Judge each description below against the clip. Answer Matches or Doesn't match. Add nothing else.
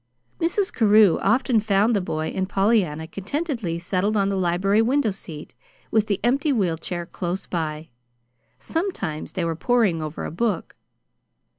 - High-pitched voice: Matches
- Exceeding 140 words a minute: Matches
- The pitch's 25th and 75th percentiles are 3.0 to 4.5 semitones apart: Doesn't match